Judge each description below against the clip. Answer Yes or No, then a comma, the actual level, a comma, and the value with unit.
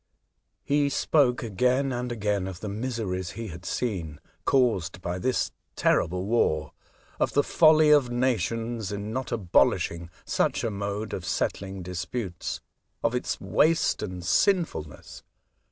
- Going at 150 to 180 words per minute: No, slow, 135 wpm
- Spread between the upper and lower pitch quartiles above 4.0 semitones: Yes, wide, 5.5 semitones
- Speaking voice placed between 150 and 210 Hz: No, low, 110 Hz